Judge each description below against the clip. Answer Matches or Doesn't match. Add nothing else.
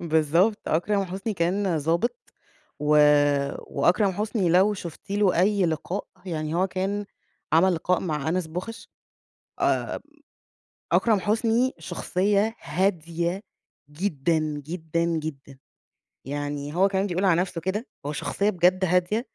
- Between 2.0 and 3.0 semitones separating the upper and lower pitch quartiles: Doesn't match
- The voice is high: Doesn't match